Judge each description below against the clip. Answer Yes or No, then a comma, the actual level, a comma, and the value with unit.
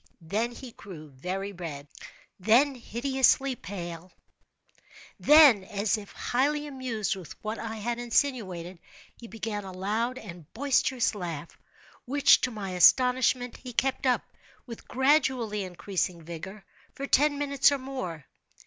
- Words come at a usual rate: No, slow, 125 wpm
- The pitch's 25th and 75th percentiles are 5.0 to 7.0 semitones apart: Yes, wide, 5.6 semitones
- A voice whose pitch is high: Yes, high, 225 Hz